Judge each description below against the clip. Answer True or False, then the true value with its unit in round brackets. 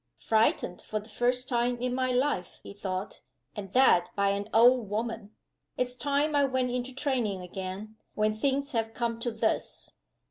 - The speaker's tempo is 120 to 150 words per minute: False (170 wpm)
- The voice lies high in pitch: True (235 Hz)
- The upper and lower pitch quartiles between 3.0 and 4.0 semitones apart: True (3.5 semitones)